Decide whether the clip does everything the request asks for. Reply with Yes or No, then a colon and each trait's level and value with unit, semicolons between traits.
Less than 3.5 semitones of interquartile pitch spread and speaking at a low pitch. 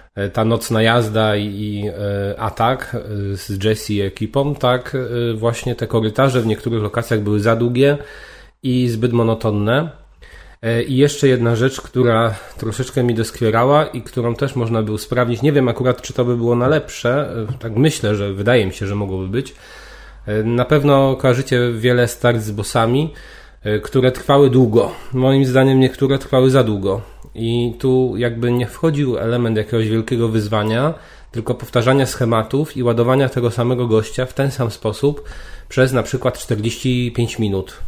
Yes: average, 2.7 semitones; low, 120 Hz